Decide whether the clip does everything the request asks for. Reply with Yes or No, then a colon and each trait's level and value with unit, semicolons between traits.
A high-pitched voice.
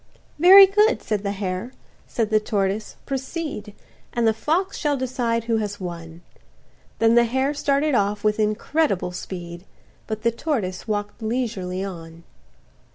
Yes: high, 220 Hz